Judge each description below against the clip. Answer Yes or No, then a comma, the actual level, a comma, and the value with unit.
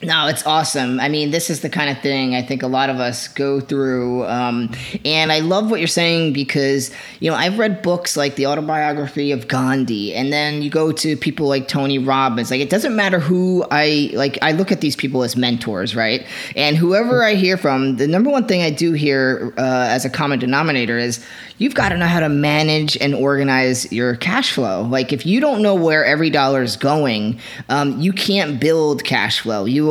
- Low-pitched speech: No, medium, 145 Hz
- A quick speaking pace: Yes, fast, 215 wpm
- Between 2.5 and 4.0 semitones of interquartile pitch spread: Yes, average, 3.5 semitones